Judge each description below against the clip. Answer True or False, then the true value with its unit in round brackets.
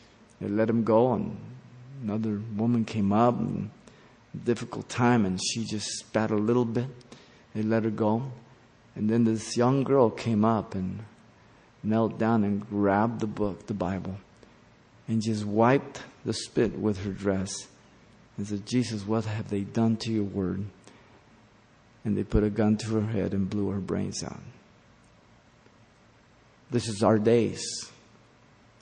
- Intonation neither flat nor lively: False (2.1 semitones)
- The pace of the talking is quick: False (155 wpm)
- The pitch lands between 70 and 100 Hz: False (110 Hz)